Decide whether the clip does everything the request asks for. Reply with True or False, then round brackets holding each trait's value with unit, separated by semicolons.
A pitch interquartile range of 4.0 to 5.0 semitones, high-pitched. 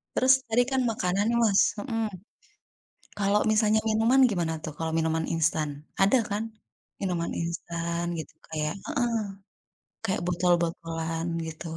False (4.7 semitones; 175 Hz)